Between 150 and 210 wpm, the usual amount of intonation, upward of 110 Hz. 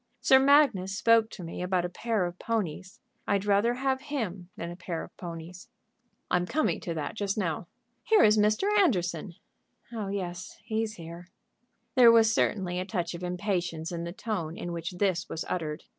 Yes: average, 180 wpm; average, 4.1 semitones; medium, 185 Hz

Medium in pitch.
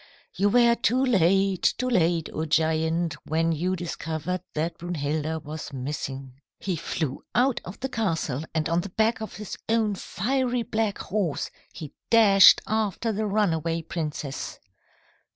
Yes: medium, 175 Hz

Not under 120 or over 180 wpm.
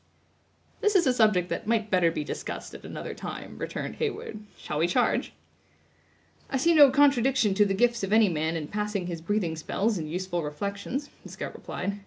No: average, 190 wpm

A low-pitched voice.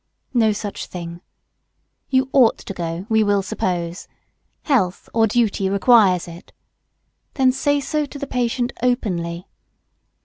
No: high, 215 Hz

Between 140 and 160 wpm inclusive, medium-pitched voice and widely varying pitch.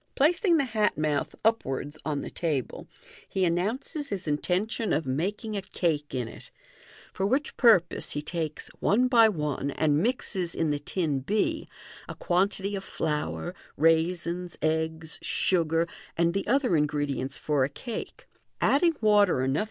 Yes: average, 150 wpm; medium, 170 Hz; wide, 5.9 semitones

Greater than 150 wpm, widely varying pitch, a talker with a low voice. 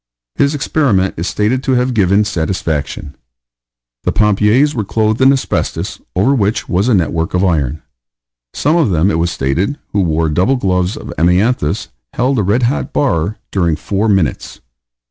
Yes: average, 165 wpm; wide, 6.4 semitones; low, 100 Hz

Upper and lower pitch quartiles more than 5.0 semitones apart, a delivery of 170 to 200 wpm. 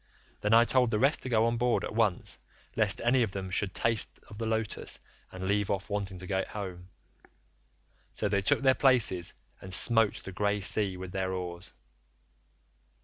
No: average, 3.2 semitones; average, 185 wpm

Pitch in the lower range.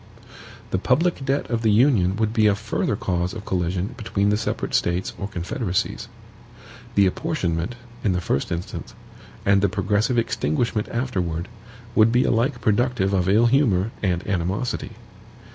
Yes: low, 105 Hz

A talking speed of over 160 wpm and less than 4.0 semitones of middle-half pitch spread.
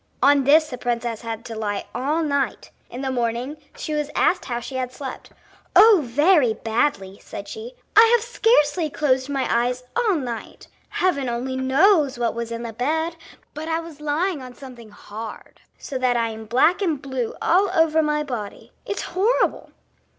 No: average, 180 wpm; average, 5.1 semitones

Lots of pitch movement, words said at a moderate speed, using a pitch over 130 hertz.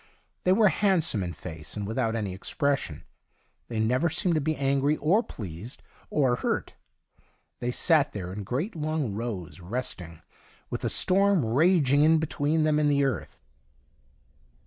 Yes: wide, 6.9 semitones; average, 150 wpm; medium, 140 Hz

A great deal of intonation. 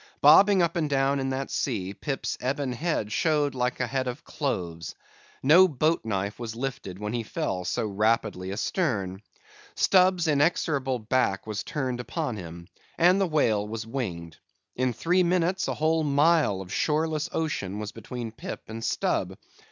Yes: wide, 6.7 semitones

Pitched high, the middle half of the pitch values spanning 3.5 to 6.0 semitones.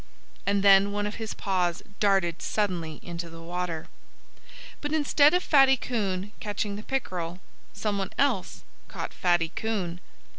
Yes: high, 200 Hz; average, 3.8 semitones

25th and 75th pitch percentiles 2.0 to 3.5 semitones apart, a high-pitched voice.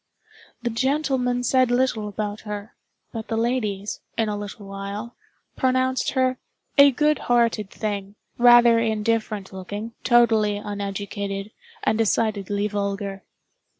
Yes: average, 3.0 semitones; high, 220 Hz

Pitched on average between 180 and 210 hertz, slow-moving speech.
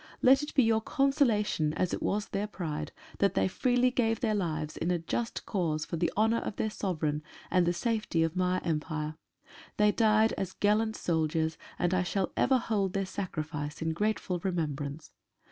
No: medium, 185 Hz; average, 180 wpm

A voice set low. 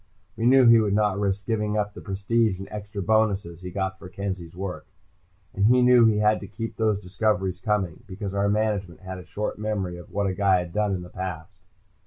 Yes: low, 100 Hz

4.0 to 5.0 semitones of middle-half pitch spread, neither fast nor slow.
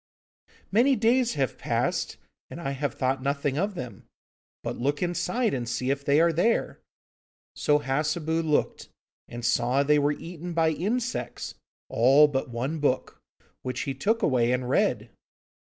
Yes: average, 4.5 semitones; average, 155 wpm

